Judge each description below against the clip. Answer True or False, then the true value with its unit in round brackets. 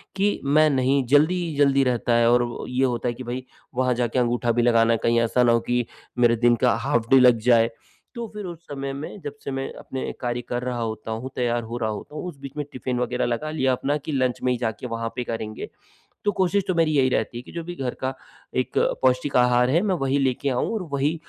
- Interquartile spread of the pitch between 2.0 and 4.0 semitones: True (2.9 semitones)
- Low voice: True (125 Hz)